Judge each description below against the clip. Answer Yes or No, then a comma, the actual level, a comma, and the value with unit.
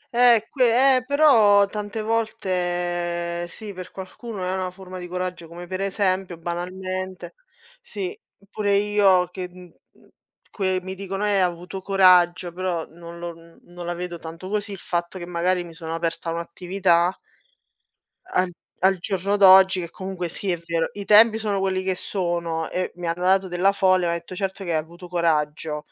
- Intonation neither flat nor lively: No, narrow, 2.2 semitones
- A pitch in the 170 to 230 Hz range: Yes, medium, 185 Hz